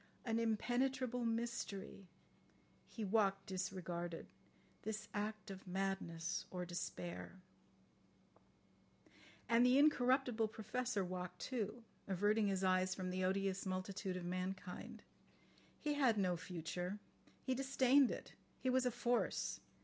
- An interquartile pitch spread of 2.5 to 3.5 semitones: No, average, 4.5 semitones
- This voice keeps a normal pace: No, slow, 120 wpm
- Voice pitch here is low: No, high, 200 Hz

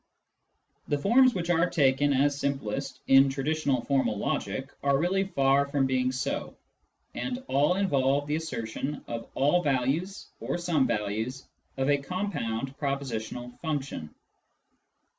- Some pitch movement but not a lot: Yes, average, 3.2 semitones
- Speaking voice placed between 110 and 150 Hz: Yes, medium, 140 Hz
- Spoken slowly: Yes, slow, 130 wpm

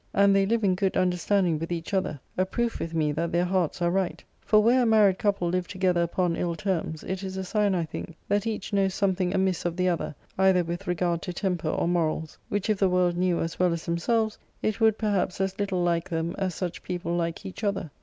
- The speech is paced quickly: Yes, fast, 235 wpm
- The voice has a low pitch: No, medium, 185 Hz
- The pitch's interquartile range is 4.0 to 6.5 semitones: No, narrow, 2.4 semitones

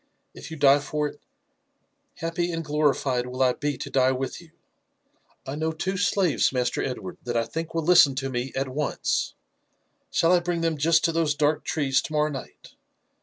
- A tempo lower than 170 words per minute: No, average, 190 wpm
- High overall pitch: No, medium, 150 Hz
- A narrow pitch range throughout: No, average, 3.7 semitones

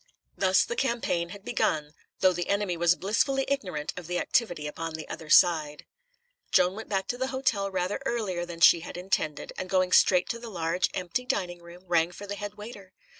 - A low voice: No, medium, 185 Hz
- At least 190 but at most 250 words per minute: Yes, average, 200 wpm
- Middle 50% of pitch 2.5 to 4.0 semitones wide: Yes, average, 3.2 semitones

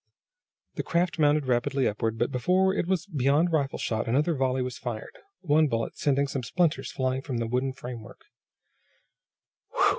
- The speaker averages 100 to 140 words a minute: No, average, 155 wpm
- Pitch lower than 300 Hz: Yes, low, 135 Hz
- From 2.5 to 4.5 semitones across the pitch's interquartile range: Yes, average, 4.0 semitones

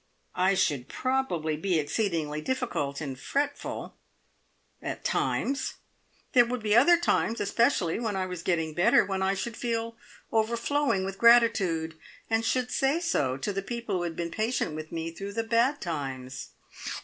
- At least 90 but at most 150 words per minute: No, average, 160 wpm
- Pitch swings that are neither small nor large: No, wide, 6.4 semitones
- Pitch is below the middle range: No, high, 200 Hz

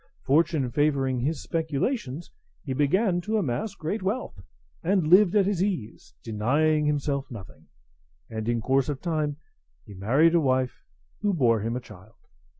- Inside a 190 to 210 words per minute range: No, average, 155 wpm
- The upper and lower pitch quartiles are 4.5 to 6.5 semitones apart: Yes, wide, 5.5 semitones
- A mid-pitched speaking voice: Yes, medium, 145 Hz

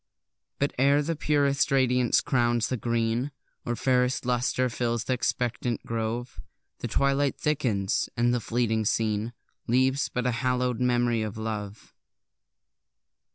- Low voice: Yes, low, 120 Hz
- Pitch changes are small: Yes, narrow, 2.2 semitones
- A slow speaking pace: Yes, slow, 130 wpm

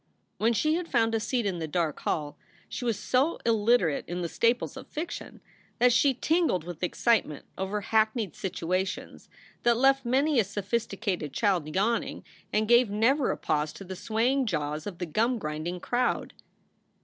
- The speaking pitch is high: Yes, high, 215 Hz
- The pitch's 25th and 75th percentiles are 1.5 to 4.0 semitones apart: No, wide, 5.4 semitones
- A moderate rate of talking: Yes, average, 175 wpm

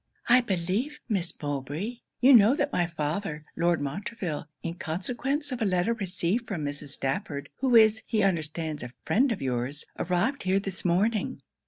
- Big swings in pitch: Yes, wide, 6.6 semitones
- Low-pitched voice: No, medium, 185 Hz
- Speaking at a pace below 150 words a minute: No, average, 165 wpm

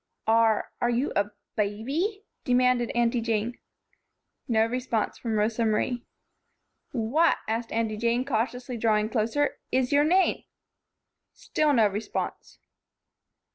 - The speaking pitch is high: Yes, high, 235 Hz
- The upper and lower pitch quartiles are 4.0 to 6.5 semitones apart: No, narrow, 2.5 semitones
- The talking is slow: Yes, slow, 115 wpm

